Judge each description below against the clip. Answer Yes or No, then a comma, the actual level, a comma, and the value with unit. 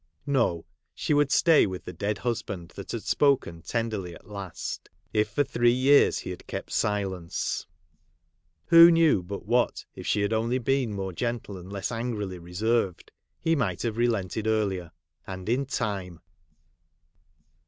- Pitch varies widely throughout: No, average, 4.6 semitones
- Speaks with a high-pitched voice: No, low, 105 Hz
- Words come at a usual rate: Yes, average, 155 wpm